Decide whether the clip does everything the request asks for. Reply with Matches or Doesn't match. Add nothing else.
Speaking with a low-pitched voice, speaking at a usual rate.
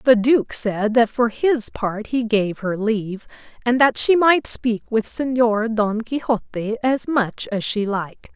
Doesn't match